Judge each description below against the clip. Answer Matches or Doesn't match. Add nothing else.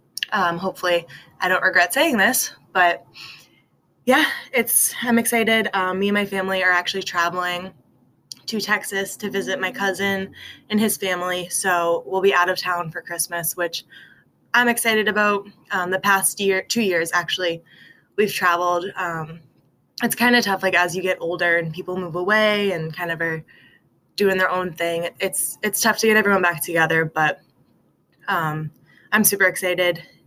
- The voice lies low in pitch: Doesn't match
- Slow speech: Doesn't match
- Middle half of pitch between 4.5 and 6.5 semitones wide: Doesn't match